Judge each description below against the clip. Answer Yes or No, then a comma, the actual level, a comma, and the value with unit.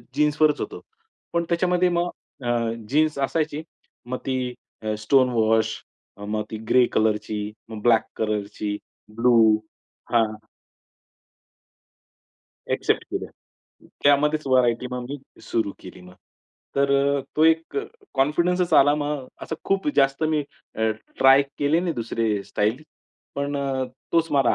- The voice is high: No, low, 135 Hz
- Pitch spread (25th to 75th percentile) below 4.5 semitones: No, average, 5.3 semitones